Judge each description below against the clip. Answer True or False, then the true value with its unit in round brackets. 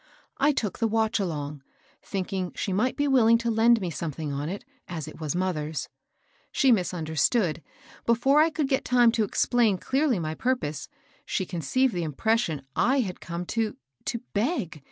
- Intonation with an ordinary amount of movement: False (6.7 semitones)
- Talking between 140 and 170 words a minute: False (180 wpm)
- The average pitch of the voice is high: True (205 Hz)